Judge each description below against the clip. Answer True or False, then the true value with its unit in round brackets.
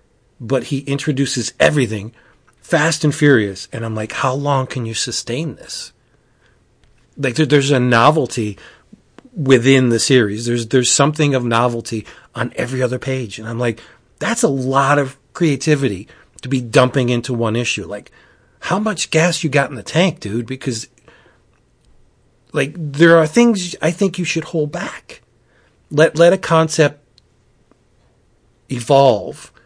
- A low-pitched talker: True (130 Hz)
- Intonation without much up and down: False (4.4 semitones)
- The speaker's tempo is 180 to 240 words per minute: False (150 wpm)